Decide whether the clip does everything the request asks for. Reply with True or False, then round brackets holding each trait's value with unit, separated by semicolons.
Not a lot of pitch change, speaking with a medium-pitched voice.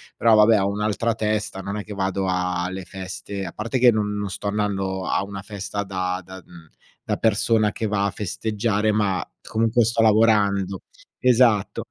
False (2.1 semitones; 100 Hz)